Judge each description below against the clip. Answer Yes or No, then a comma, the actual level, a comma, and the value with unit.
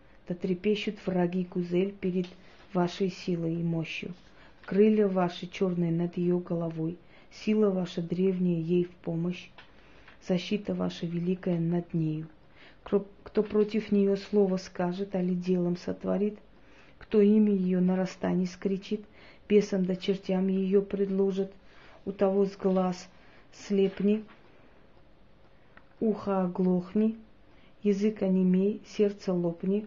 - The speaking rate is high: No, average, 115 wpm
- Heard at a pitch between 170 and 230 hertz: Yes, medium, 185 Hz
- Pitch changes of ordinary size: No, narrow, 2.2 semitones